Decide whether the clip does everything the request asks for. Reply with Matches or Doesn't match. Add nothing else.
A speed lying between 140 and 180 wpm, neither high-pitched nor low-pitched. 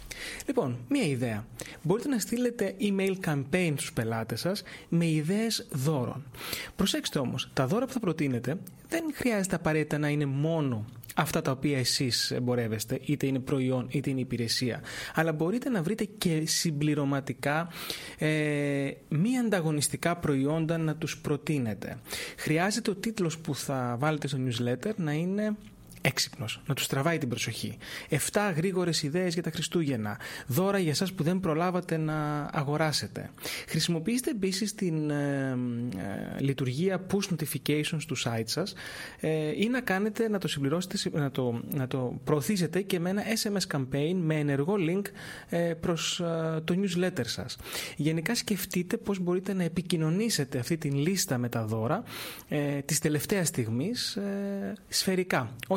Matches